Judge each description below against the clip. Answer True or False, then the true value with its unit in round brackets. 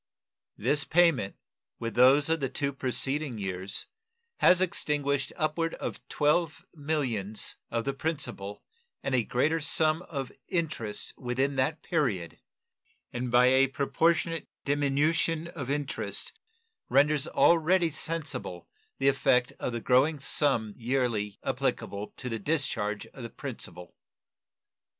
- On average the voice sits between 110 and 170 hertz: True (140 Hz)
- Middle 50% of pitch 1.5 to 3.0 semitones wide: False (4.3 semitones)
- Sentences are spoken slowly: True (120 wpm)